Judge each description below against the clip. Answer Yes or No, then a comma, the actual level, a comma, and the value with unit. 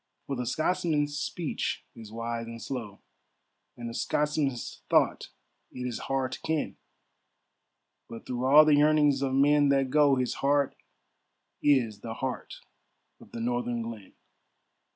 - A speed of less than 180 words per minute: Yes, average, 140 wpm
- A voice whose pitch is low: Yes, low, 130 Hz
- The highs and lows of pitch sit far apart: No, average, 3.8 semitones